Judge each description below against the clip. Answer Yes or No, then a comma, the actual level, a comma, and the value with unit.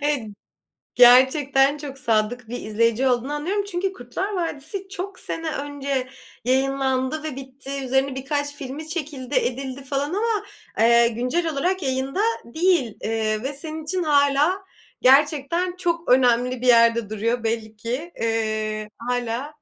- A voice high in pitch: Yes, very high, 270 Hz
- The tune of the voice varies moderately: Yes, average, 4.2 semitones